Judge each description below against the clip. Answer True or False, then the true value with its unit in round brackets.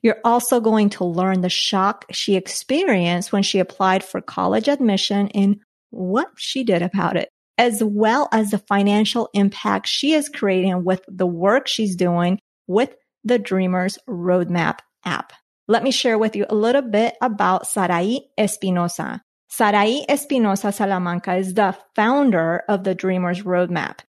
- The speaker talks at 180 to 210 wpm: False (150 wpm)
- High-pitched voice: True (200 Hz)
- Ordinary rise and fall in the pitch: True (3.3 semitones)